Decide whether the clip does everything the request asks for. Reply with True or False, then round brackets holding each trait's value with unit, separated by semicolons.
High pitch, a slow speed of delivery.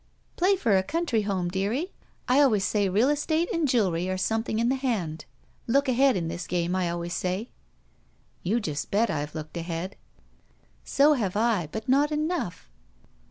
False (215 Hz; 170 wpm)